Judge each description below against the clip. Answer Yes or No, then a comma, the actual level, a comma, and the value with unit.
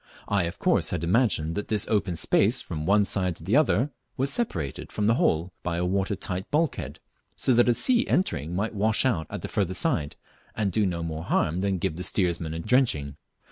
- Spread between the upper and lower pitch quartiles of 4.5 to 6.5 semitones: Yes, average, 5.1 semitones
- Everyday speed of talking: No, fast, 215 wpm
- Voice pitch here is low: Yes, very low, 95 Hz